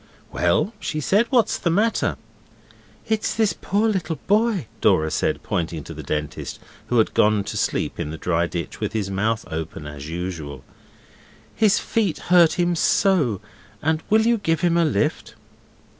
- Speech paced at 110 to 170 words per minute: Yes, average, 165 wpm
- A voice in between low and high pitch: Yes, medium, 155 Hz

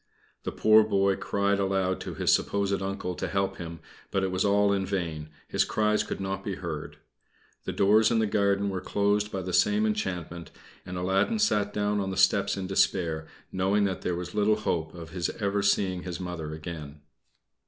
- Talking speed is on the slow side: No, average, 195 wpm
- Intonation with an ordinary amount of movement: No, narrow, 2.2 semitones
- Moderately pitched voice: No, very low, 95 Hz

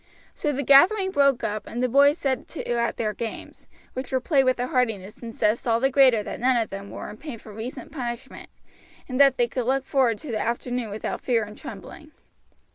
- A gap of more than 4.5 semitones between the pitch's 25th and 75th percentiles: No, average, 3.1 semitones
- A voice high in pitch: Yes, very high, 250 Hz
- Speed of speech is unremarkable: No, fast, 220 wpm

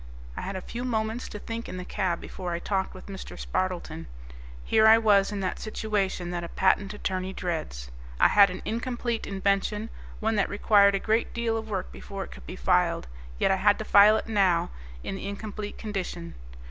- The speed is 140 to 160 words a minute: No, average, 200 wpm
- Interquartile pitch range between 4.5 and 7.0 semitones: No, average, 2.7 semitones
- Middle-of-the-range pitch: No, high, 200 Hz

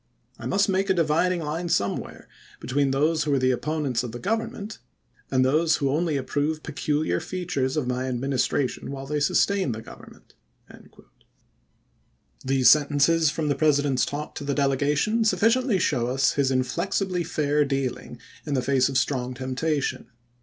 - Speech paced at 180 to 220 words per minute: No, average, 160 wpm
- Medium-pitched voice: Yes, medium, 145 Hz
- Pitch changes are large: No, average, 3.9 semitones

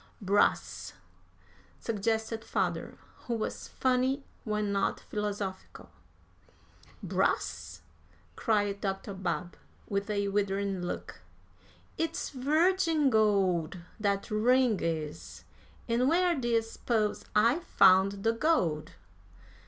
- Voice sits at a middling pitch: No, high, 210 Hz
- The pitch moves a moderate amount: Yes, average, 4.1 semitones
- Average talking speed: No, slow, 95 wpm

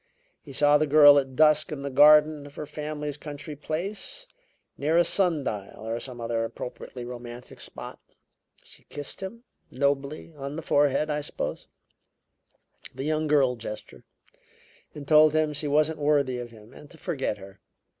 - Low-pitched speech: No, medium, 145 Hz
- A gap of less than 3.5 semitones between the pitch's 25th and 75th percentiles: Yes, average, 2.7 semitones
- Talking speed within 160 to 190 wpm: Yes, average, 165 wpm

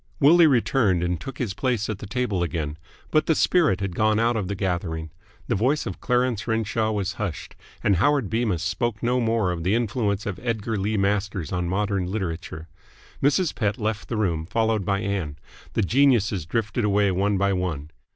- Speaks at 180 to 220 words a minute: Yes, average, 190 wpm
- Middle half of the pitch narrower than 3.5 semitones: No, average, 4.0 semitones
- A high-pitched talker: No, low, 105 Hz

